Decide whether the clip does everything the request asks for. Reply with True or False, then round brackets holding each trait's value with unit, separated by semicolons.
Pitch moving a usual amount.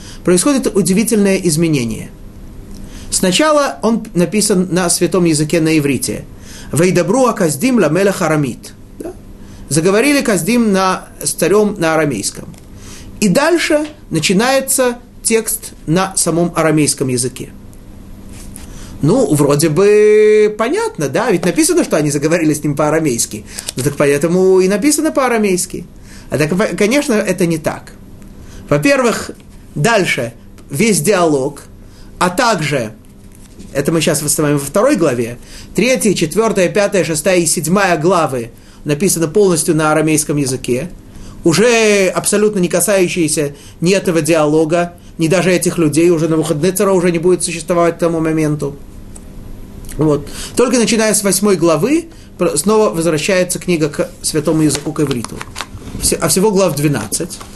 False (5.7 semitones)